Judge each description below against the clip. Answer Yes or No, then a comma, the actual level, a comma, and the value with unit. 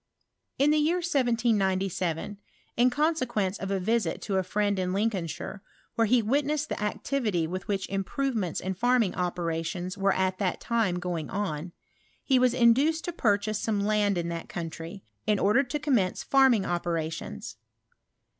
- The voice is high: Yes, high, 205 Hz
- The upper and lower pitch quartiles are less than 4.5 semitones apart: No, average, 5.1 semitones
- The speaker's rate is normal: Yes, average, 165 wpm